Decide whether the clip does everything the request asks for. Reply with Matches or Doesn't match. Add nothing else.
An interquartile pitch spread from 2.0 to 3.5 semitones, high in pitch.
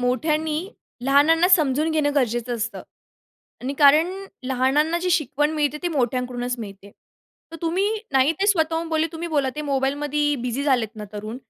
Doesn't match